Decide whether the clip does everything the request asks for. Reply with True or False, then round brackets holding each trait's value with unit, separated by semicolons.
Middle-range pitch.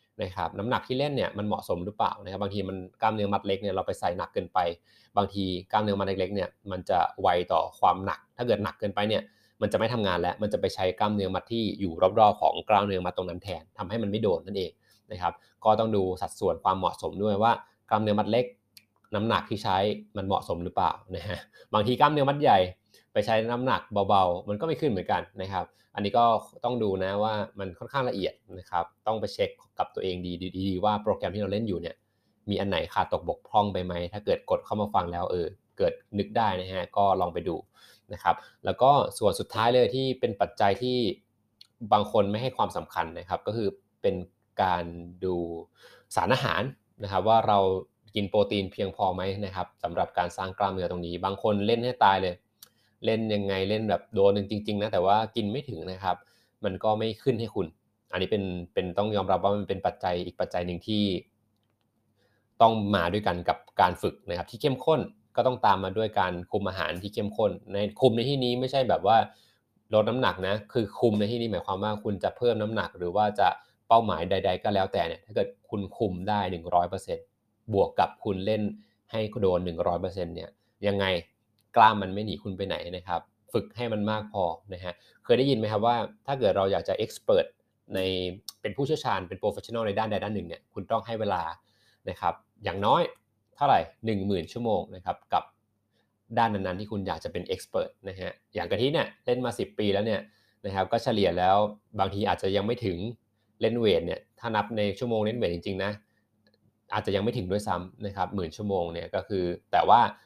False (105 Hz)